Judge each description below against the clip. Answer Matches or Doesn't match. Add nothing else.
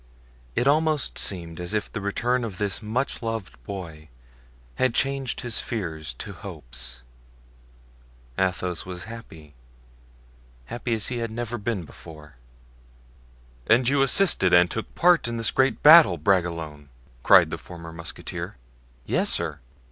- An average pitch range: Doesn't match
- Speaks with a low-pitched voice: Matches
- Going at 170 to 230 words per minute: Doesn't match